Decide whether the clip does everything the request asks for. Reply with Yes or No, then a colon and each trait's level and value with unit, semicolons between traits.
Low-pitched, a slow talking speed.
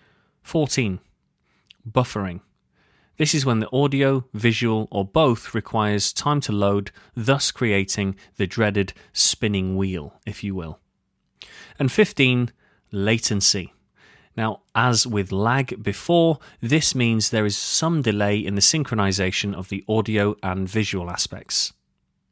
Yes: low, 110 Hz; slow, 125 wpm